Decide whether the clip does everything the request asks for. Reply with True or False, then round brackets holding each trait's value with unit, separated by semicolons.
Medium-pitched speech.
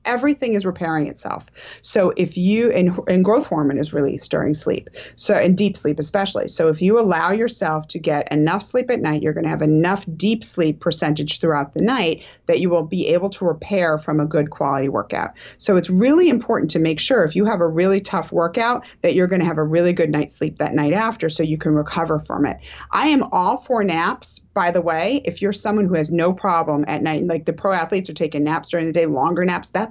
True (170 Hz)